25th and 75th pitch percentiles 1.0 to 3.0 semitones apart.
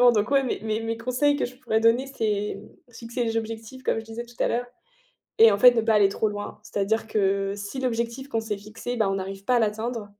Yes: narrow, 2.6 semitones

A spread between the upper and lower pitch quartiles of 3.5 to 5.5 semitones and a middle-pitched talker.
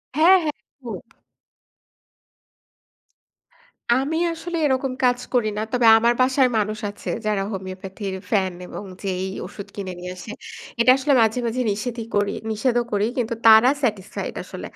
No: average, 4.0 semitones; high, 220 Hz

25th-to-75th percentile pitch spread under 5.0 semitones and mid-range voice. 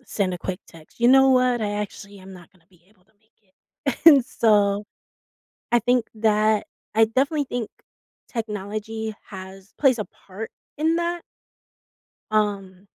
No: average, 3.5 semitones; high, 215 Hz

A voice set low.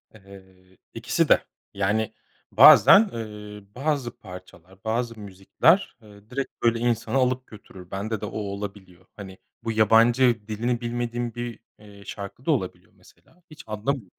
Yes: low, 110 Hz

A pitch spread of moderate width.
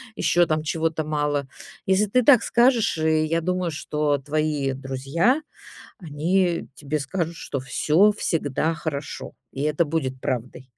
Yes: average, 3.3 semitones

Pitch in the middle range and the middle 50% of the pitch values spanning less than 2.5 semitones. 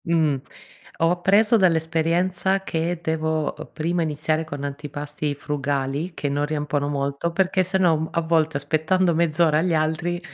No: medium, 160 Hz; average, 2.8 semitones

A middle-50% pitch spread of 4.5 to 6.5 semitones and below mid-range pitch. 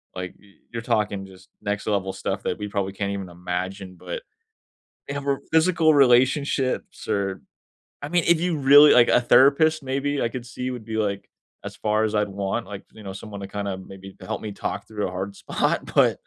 Yes: wide, 5.6 semitones; low, 105 Hz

